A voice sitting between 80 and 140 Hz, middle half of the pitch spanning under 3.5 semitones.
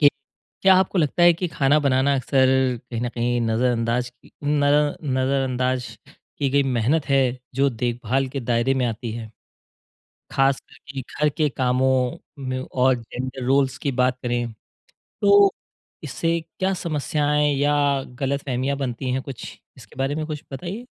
Yes: low, 135 Hz; average, 2.8 semitones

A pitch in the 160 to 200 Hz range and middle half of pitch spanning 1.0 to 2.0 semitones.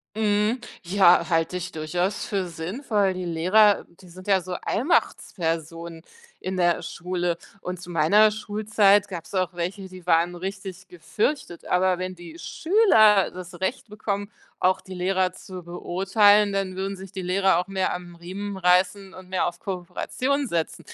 No: medium, 185 Hz; narrow, 2.5 semitones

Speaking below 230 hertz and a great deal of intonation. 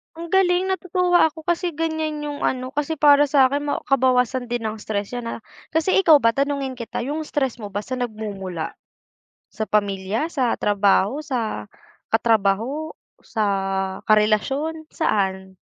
No: very high, 255 Hz; wide, 6.3 semitones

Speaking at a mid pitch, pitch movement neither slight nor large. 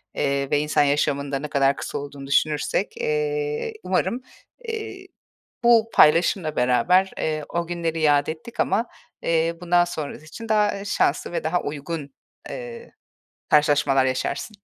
No: medium, 160 Hz; wide, 6.5 semitones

